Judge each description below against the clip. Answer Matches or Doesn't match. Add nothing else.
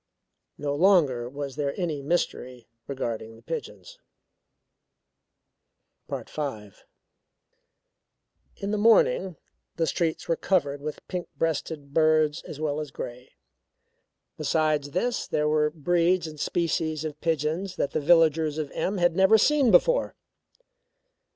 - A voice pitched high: Doesn't match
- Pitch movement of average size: Matches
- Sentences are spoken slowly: Matches